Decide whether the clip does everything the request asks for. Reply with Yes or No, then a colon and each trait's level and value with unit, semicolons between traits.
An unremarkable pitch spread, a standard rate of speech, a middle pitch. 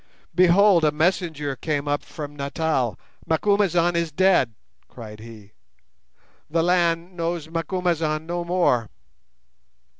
No: average, 3.1 semitones; slow, 110 wpm; medium, 165 Hz